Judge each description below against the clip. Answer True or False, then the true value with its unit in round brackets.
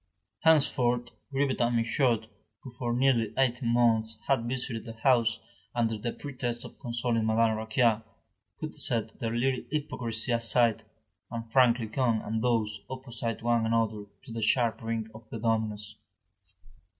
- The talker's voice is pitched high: False (115 Hz)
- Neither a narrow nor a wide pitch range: False (1.7 semitones)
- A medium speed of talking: True (145 wpm)